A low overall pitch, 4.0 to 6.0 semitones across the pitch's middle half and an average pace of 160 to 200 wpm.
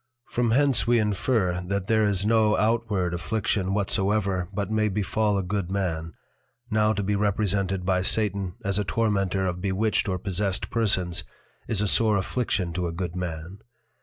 No: low, 100 Hz; average, 2.7 semitones; average, 170 wpm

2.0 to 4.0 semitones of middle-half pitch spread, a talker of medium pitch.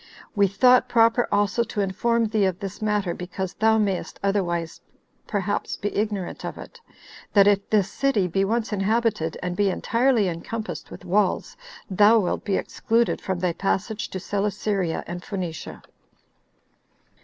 No: average, 2.8 semitones; high, 200 Hz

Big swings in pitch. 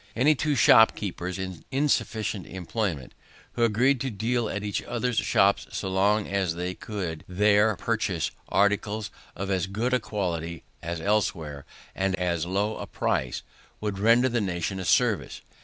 No: average, 3.5 semitones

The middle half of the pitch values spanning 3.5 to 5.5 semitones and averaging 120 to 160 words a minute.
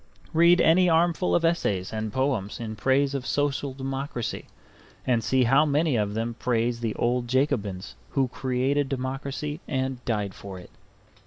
Yes: average, 3.8 semitones; average, 155 wpm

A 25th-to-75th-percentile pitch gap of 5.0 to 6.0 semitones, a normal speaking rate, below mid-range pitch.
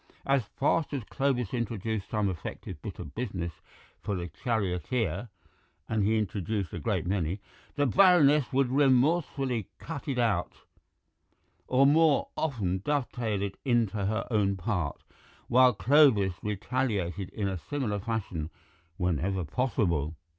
No: wide, 5.5 semitones; slow, 130 wpm; low, 110 Hz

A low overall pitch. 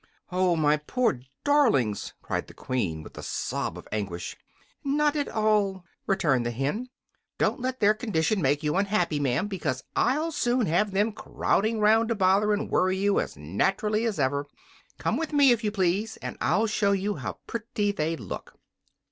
No: high, 200 Hz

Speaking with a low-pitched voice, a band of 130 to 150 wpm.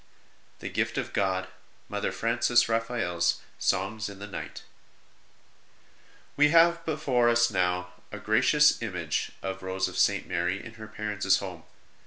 Yes: low, 105 Hz; average, 145 wpm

